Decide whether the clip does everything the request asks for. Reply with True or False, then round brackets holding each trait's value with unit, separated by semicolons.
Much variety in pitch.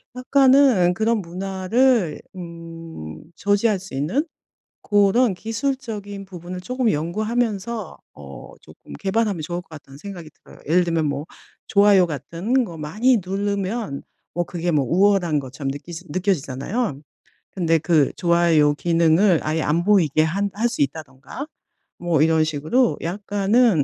False (4.8 semitones)